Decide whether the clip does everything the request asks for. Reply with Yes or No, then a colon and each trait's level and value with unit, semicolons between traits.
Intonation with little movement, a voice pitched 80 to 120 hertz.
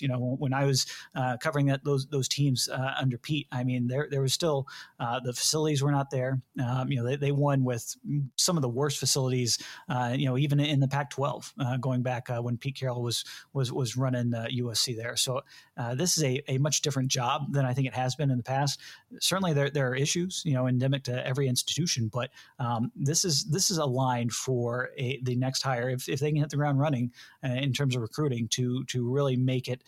No: narrow, 2.3 semitones; low, 130 Hz